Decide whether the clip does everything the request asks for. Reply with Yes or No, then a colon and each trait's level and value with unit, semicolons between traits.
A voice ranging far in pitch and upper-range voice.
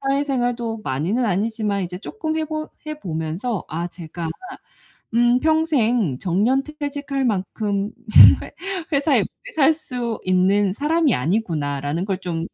Yes: wide, 7.5 semitones; high, 225 Hz